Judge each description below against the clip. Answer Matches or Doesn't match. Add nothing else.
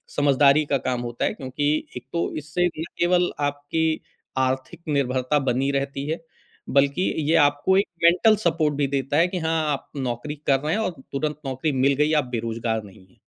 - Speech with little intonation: Doesn't match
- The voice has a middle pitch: Matches